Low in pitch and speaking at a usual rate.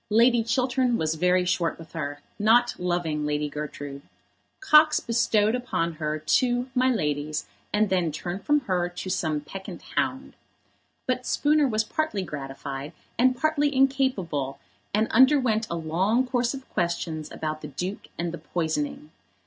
No: medium, 185 Hz; average, 150 wpm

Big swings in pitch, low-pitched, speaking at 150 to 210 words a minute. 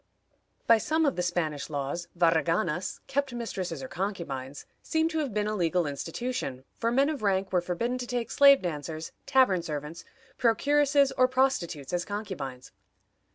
No: wide, 7.7 semitones; high, 190 Hz; average, 155 wpm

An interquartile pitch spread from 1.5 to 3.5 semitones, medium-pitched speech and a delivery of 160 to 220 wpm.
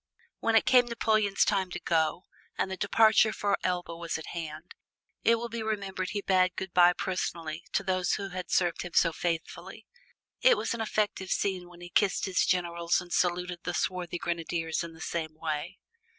Yes: average, 2.7 semitones; medium, 180 Hz; average, 190 wpm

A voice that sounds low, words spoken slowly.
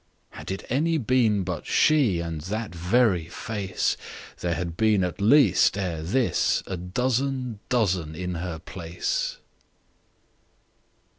Yes: very low, 95 Hz; slow, 105 wpm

